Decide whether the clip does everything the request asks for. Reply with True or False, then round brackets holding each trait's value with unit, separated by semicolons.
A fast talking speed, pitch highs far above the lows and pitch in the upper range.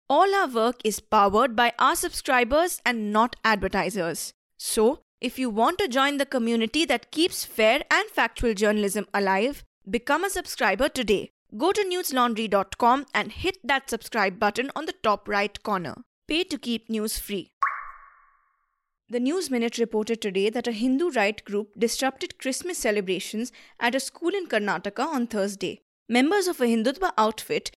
False (160 wpm; 6.4 semitones; 245 Hz)